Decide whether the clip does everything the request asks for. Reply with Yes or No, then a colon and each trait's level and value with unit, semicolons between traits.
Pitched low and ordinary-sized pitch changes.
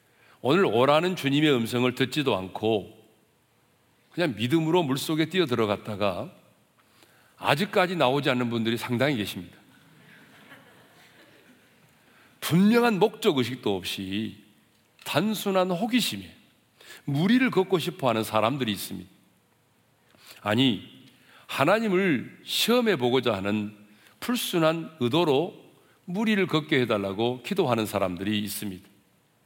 No: low, 125 Hz; wide, 9.0 semitones